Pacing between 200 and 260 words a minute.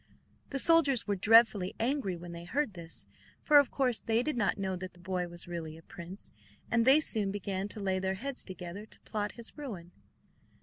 Yes: fast, 205 wpm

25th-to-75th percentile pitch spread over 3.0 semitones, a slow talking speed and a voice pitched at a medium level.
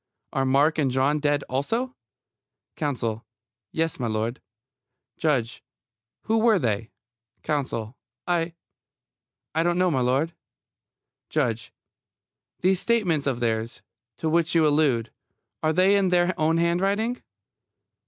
Yes: wide, 5.5 semitones; slow, 115 wpm; medium, 155 Hz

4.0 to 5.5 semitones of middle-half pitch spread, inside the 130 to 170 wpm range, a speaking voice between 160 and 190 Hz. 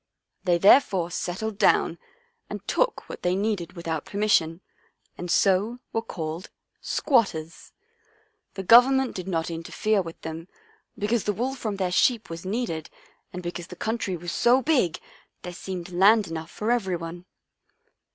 Yes: average, 4.4 semitones; average, 150 wpm; medium, 185 Hz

